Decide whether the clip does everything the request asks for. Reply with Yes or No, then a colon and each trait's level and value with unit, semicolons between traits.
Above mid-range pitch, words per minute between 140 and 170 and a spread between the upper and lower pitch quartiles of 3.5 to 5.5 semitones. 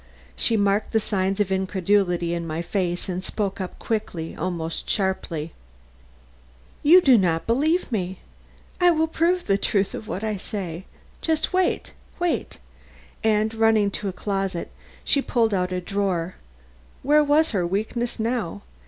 Yes: high, 200 Hz; average, 145 wpm; average, 3.8 semitones